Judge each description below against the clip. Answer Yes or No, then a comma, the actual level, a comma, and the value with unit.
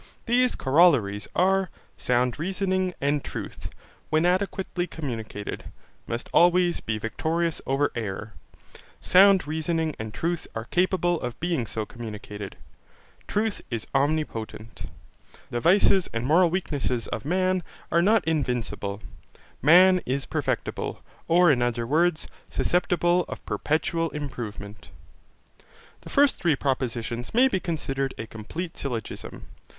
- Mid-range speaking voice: Yes, medium, 155 Hz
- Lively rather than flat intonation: Yes, wide, 6.9 semitones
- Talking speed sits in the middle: No, slow, 120 wpm